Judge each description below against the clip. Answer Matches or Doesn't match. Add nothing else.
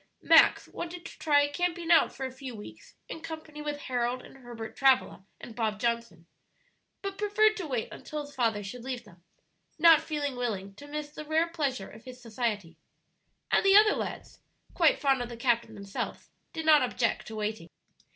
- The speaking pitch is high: Matches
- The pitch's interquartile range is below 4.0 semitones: Doesn't match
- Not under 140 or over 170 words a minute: Doesn't match